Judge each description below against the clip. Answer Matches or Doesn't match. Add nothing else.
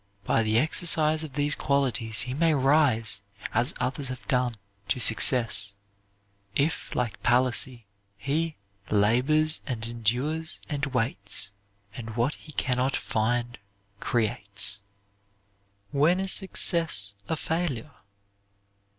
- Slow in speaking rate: Matches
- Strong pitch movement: Doesn't match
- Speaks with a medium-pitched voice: Doesn't match